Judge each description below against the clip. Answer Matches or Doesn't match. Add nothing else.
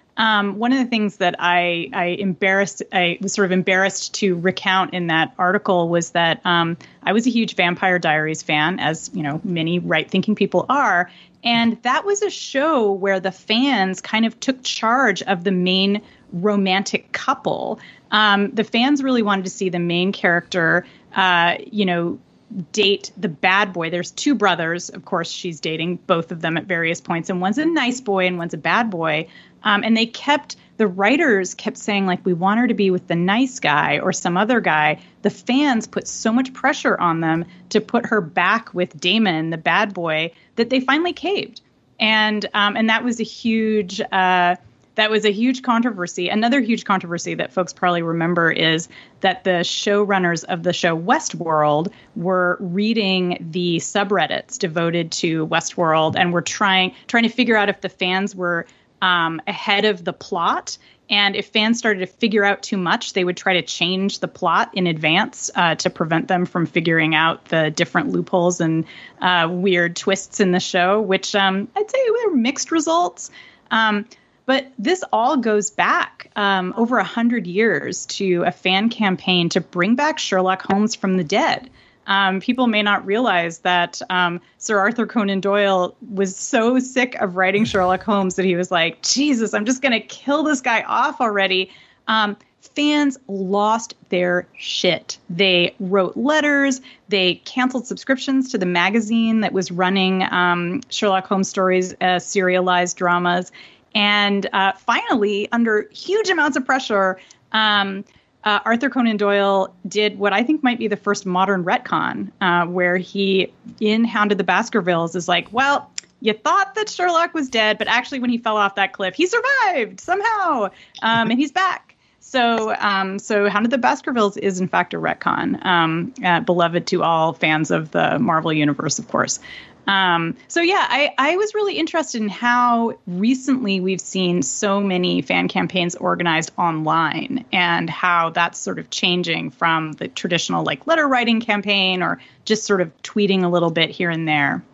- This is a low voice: Doesn't match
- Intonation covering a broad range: Doesn't match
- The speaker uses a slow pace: Doesn't match